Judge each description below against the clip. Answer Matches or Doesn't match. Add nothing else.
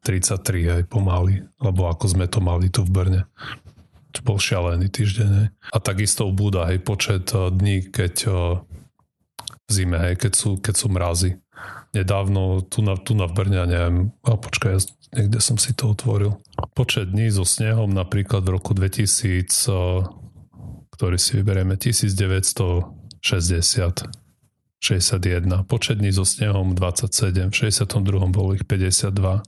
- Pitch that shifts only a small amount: Doesn't match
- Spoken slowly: Doesn't match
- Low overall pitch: Matches